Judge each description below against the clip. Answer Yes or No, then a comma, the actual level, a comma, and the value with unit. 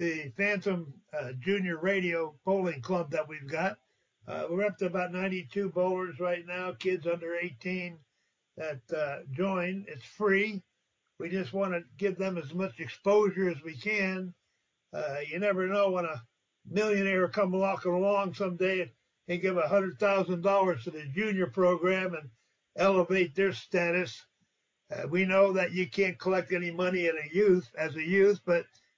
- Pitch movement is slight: Yes, narrow, 2.2 semitones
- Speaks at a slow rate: No, average, 165 wpm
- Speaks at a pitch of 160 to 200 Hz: Yes, medium, 185 Hz